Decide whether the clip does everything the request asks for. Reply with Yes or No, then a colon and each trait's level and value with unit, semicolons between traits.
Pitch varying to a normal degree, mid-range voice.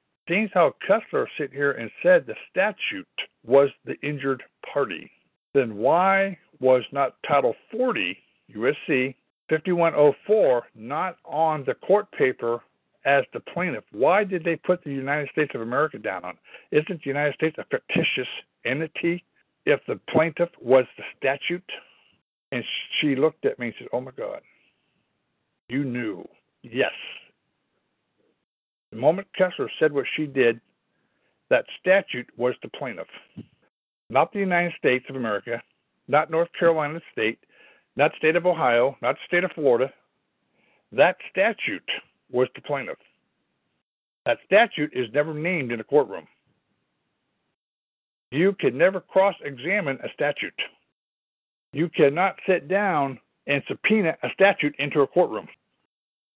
Yes: average, 4.6 semitones; medium, 150 Hz